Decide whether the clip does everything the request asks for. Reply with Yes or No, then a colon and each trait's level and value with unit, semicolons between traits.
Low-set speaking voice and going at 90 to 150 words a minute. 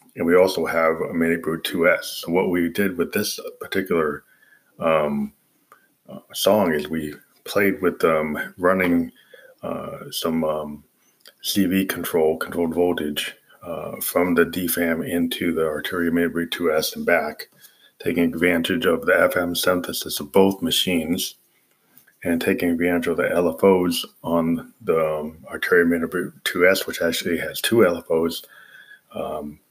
Yes: very low, 85 Hz; slow, 135 wpm